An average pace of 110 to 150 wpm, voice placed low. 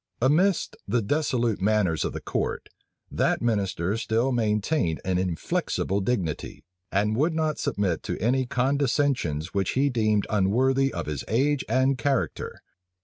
Yes: average, 140 wpm; low, 115 Hz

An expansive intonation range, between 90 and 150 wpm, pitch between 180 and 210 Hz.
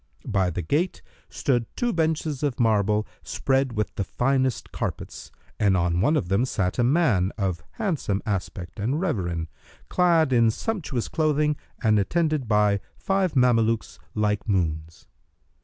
No: wide, 7.2 semitones; average, 140 wpm; low, 115 Hz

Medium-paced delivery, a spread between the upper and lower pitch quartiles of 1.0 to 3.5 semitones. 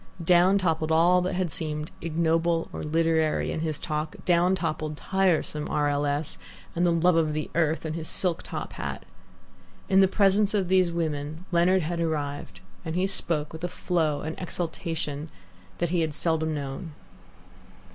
Yes: average, 170 wpm; narrow, 2.5 semitones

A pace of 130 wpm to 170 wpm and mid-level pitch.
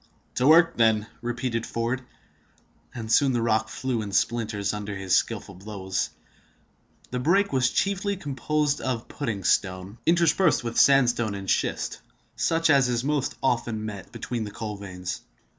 No: average, 155 wpm; low, 120 Hz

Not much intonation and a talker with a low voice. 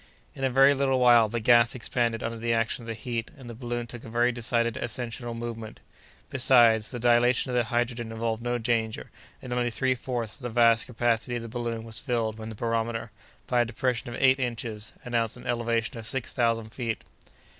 Yes: narrow, 1.2 semitones; low, 120 Hz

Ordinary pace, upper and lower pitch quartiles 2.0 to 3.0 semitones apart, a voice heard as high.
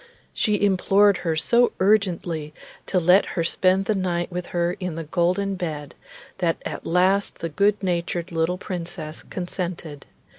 No: average, 150 wpm; narrow, 2.6 semitones; medium, 180 Hz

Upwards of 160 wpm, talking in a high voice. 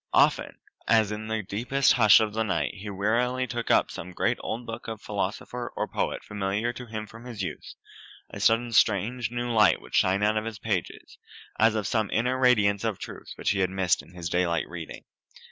No: fast, 205 wpm; low, 110 Hz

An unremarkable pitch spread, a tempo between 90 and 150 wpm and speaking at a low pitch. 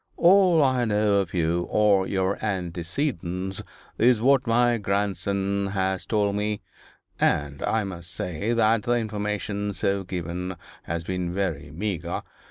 Yes: average, 3.0 semitones; slow, 135 wpm; low, 100 Hz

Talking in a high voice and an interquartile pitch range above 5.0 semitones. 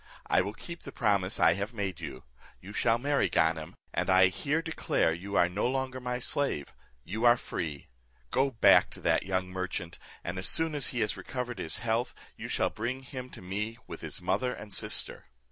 No: low, 105 Hz; wide, 5.4 semitones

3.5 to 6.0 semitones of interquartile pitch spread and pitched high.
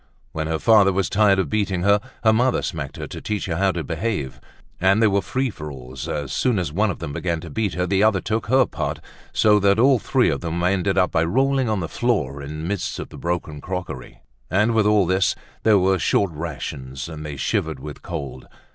No: average, 5.2 semitones; very low, 95 Hz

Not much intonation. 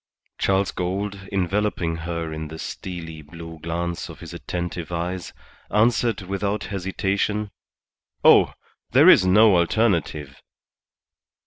No: average, 3.1 semitones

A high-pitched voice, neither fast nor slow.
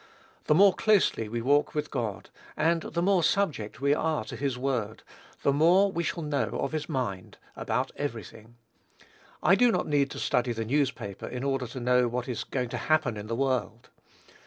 No: low, 135 Hz; average, 195 wpm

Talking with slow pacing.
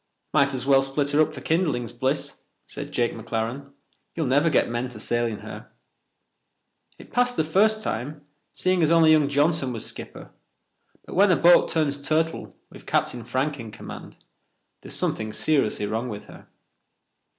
No: average, 170 wpm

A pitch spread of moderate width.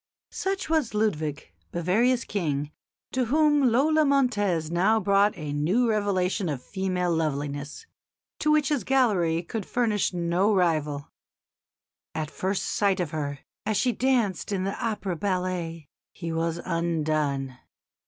No: wide, 5.7 semitones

